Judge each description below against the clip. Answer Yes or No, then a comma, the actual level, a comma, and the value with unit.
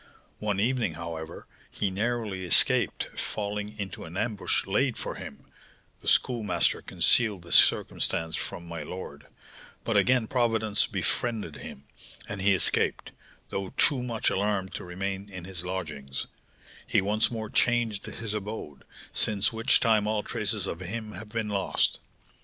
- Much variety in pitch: No, average, 3.3 semitones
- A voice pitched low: Yes, low, 105 Hz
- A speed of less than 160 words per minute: Yes, average, 145 wpm